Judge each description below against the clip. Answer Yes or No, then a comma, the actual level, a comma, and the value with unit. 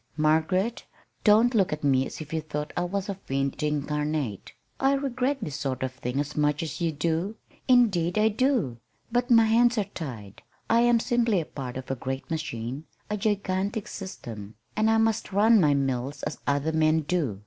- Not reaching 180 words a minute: No, average, 190 wpm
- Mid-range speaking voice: Yes, medium, 160 Hz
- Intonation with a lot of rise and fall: Yes, wide, 7.5 semitones